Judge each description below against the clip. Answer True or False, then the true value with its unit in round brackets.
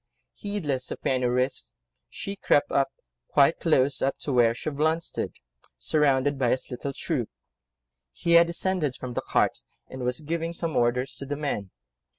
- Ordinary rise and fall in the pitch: True (4.1 semitones)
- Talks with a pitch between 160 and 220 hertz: False (140 Hz)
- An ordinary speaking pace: True (160 wpm)